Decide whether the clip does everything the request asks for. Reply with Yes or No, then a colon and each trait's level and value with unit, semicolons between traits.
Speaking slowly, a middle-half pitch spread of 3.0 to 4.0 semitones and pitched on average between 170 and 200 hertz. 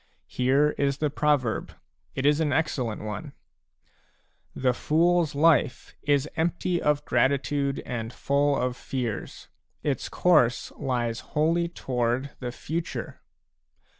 No: slow, 125 wpm; average, 3.4 semitones; medium, 140 Hz